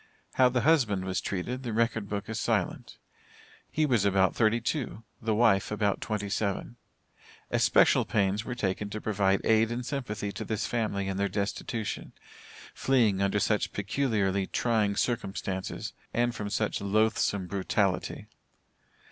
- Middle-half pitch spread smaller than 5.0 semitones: Yes, average, 2.8 semitones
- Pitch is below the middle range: Yes, low, 105 Hz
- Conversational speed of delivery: Yes, average, 145 wpm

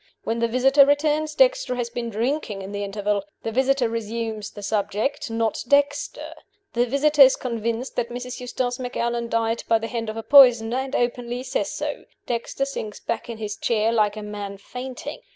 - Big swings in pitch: No, average, 3.0 semitones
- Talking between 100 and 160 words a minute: No, average, 185 wpm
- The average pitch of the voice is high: Yes, high, 235 Hz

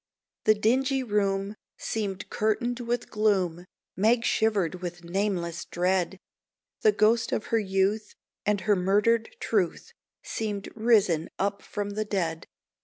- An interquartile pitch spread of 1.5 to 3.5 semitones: Yes, average, 2.8 semitones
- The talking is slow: Yes, slow, 125 wpm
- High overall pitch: Yes, high, 205 Hz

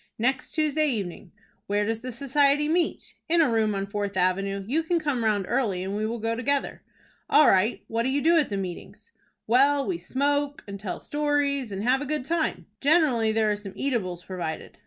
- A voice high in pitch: Yes, high, 240 Hz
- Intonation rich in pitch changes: Yes, wide, 6.1 semitones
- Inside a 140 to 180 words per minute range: No, average, 200 wpm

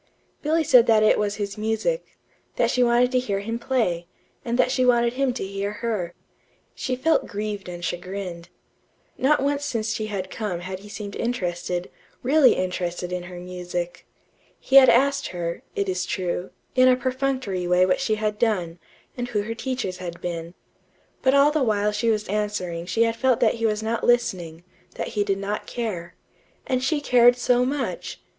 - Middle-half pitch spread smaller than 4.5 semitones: No, wide, 5.4 semitones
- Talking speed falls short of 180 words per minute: No, average, 185 wpm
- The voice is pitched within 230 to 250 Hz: No, high, 215 Hz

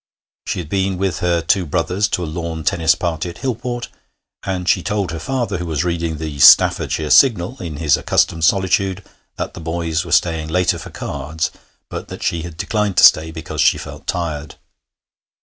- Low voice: Yes, very low, 85 Hz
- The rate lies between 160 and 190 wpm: Yes, average, 185 wpm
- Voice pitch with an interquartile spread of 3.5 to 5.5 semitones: No, average, 3.0 semitones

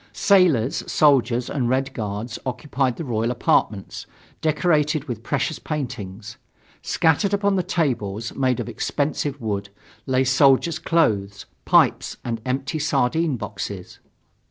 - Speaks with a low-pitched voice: Yes, low, 130 Hz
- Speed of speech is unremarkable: No, slow, 120 wpm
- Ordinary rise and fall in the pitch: Yes, average, 5.0 semitones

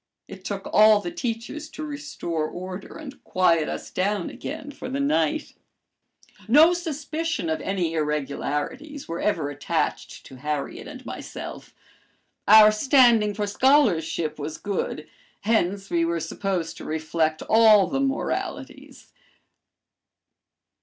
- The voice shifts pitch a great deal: Yes, wide, 8.8 semitones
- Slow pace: Yes, slow, 125 wpm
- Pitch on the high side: Yes, high, 205 Hz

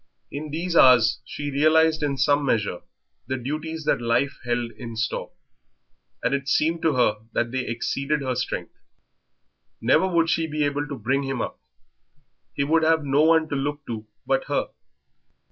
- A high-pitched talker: No, medium, 140 Hz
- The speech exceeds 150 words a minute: Yes, average, 170 wpm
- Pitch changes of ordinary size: Yes, average, 3.8 semitones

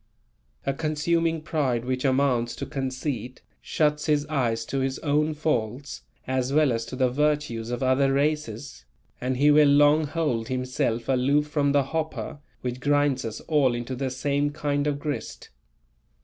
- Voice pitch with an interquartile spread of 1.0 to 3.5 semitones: Yes, average, 2.7 semitones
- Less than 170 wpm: Yes, average, 160 wpm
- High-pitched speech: No, medium, 140 Hz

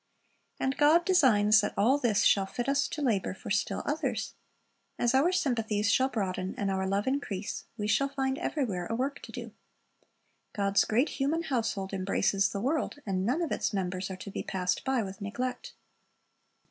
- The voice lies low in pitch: No, high, 220 Hz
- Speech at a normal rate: Yes, average, 180 wpm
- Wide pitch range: Yes, wide, 5.7 semitones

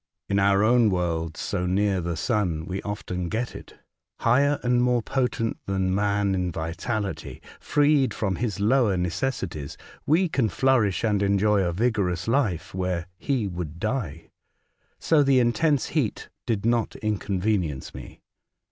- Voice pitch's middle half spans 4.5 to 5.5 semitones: Yes, average, 4.9 semitones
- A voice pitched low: Yes, low, 100 Hz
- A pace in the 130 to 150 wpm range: Yes, average, 145 wpm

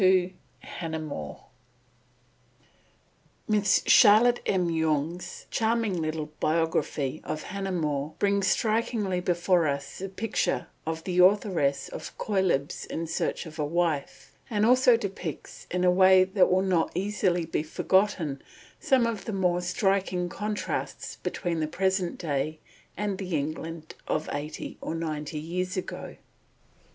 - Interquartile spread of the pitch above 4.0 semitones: No, average, 3.7 semitones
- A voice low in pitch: No, medium, 180 Hz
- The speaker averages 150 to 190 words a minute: No, slow, 135 wpm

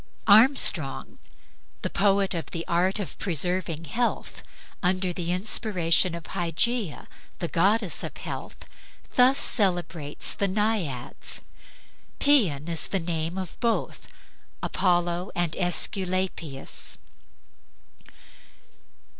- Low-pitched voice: No, medium, 180 Hz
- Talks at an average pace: No, slow, 95 wpm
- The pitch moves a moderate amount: Yes, average, 3.2 semitones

